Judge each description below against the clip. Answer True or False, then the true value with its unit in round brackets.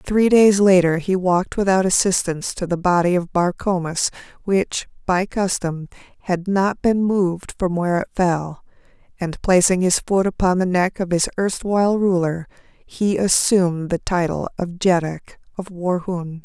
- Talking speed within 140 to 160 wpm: True (155 wpm)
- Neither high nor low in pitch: True (180 Hz)